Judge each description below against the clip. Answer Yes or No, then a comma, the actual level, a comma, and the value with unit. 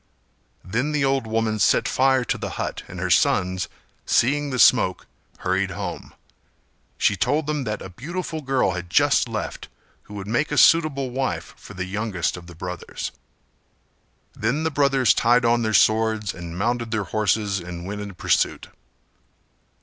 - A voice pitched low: Yes, low, 115 Hz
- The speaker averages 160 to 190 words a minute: Yes, average, 165 wpm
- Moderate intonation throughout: No, wide, 5.7 semitones